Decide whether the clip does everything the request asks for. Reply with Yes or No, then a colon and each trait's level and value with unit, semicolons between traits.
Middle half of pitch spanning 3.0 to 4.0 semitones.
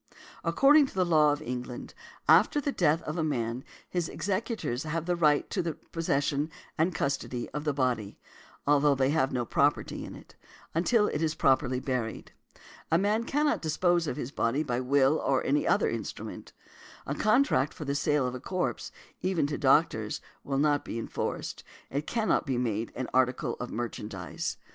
No: average, 4.5 semitones